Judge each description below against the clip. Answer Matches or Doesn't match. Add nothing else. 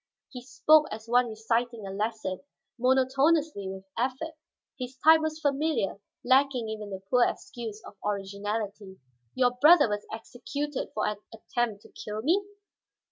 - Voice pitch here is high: Matches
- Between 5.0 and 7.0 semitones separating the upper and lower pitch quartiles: Doesn't match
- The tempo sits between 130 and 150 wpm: Matches